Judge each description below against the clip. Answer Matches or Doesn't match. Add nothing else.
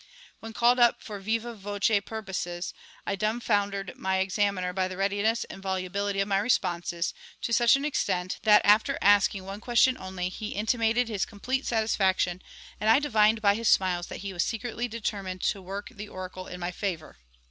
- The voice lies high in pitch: Matches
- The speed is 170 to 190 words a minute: Matches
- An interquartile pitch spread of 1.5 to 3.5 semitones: Matches